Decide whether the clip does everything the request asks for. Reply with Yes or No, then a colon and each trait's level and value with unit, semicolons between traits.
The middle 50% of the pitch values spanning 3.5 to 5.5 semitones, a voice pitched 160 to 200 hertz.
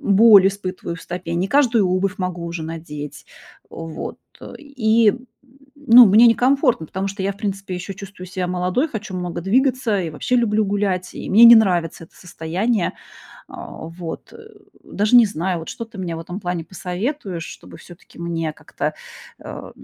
Yes: average, 4.2 semitones; high, 190 Hz